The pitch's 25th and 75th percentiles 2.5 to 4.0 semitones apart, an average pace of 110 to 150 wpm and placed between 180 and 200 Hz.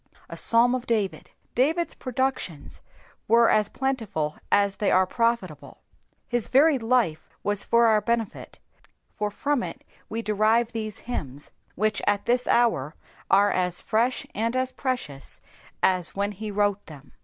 No: average, 3.6 semitones; average, 145 wpm; high, 215 Hz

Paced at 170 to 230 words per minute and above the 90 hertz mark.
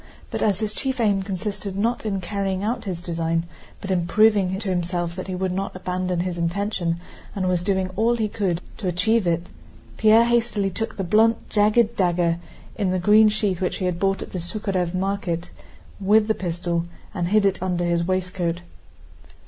Yes: average, 190 wpm; high, 190 Hz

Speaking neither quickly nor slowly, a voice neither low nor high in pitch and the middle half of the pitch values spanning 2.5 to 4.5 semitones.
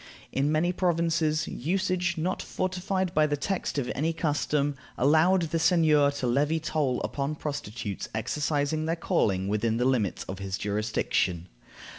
No: average, 145 wpm; medium, 150 Hz; average, 5.2 semitones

